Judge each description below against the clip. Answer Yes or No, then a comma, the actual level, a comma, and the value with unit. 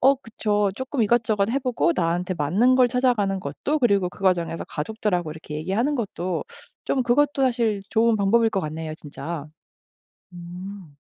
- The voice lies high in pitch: Yes, high, 205 Hz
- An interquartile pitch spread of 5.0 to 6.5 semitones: Yes, wide, 5.6 semitones